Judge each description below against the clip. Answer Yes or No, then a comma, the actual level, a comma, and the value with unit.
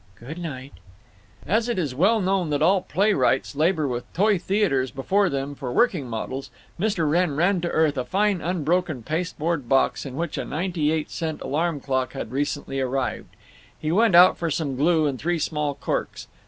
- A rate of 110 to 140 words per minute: No, average, 180 wpm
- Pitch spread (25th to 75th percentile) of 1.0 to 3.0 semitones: No, average, 4.7 semitones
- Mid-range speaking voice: Yes, medium, 160 Hz